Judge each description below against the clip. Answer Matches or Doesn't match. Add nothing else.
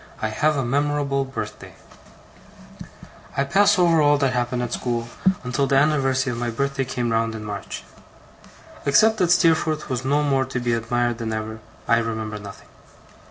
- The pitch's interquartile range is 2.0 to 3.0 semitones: Doesn't match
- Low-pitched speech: Matches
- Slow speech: Doesn't match